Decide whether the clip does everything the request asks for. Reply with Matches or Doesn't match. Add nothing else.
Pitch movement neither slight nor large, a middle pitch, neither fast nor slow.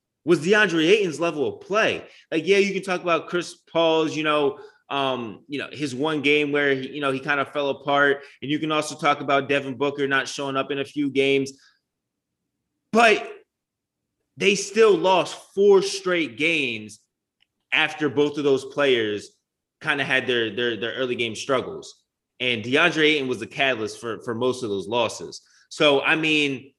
Matches